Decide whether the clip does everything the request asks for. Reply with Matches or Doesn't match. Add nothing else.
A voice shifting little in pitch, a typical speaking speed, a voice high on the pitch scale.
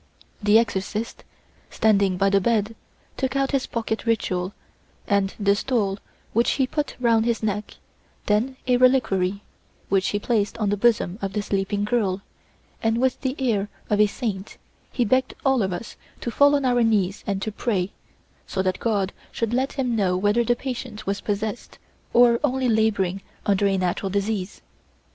Doesn't match